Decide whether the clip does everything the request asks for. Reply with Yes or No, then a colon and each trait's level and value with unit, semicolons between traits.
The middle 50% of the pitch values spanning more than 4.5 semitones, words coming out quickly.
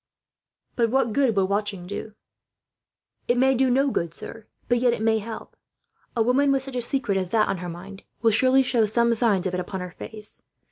No: average, 4.1 semitones; fast, 215 wpm